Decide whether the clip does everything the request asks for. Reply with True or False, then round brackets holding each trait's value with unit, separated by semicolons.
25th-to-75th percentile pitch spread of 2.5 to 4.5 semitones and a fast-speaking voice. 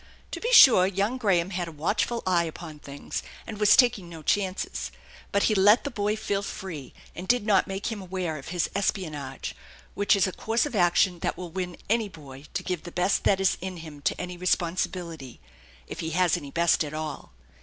True (3.5 semitones; 210 wpm)